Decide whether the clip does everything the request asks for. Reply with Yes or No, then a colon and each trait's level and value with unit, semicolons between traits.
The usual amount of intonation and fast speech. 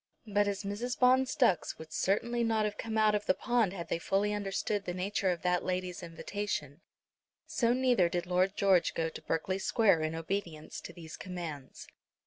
No: average, 3.6 semitones; average, 185 wpm